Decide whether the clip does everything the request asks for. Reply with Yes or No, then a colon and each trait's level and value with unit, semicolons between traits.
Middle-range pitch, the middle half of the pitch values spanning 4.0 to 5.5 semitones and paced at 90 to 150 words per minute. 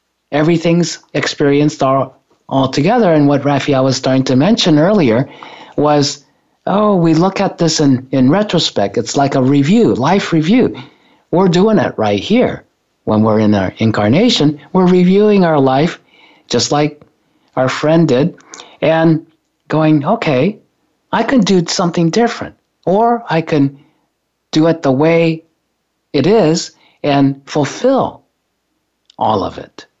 Yes: medium, 155 Hz; average, 4.6 semitones; average, 140 wpm